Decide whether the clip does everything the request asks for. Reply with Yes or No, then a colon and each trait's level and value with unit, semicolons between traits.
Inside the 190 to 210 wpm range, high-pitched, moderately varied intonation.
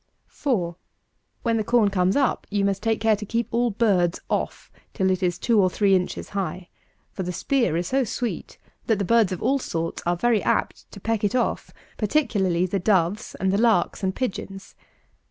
Yes: average, 195 wpm; high, 200 Hz; average, 3.9 semitones